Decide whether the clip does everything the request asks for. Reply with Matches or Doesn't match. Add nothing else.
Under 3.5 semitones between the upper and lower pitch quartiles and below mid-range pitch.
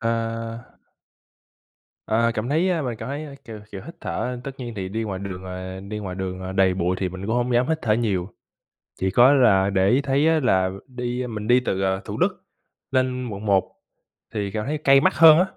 Doesn't match